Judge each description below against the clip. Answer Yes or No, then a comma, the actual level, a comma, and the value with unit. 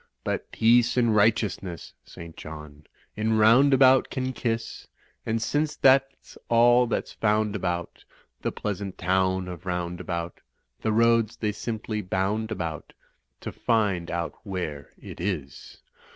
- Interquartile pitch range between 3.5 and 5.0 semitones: Yes, average, 4.6 semitones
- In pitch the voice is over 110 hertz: No, low, 105 Hz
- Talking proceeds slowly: Yes, slow, 125 wpm